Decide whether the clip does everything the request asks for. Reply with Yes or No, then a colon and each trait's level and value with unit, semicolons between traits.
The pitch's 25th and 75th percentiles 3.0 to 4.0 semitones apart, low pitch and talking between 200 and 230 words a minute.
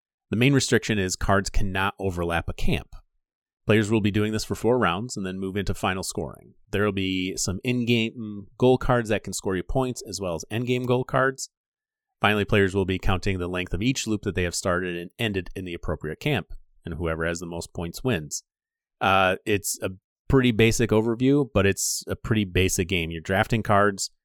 Yes: average, 3.7 semitones; low, 100 Hz; fast, 205 wpm